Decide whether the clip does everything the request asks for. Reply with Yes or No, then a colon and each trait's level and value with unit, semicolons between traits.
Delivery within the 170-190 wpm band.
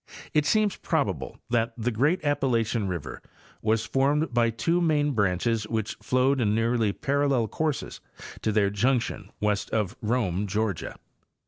No: average, 140 wpm